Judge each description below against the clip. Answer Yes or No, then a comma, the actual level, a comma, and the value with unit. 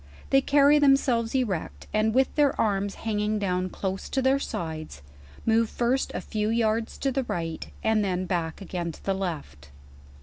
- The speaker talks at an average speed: Yes, average, 170 wpm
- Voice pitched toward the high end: Yes, high, 215 Hz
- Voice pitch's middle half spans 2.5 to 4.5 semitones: No, wide, 5.6 semitones